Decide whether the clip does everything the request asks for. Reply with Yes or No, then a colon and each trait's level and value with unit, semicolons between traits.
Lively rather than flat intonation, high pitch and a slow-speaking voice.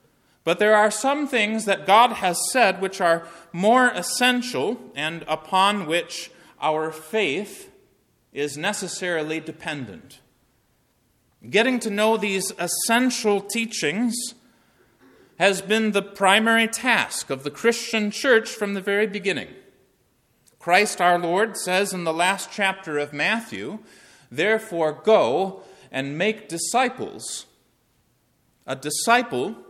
No: average, 4.6 semitones; high, 200 Hz; slow, 115 wpm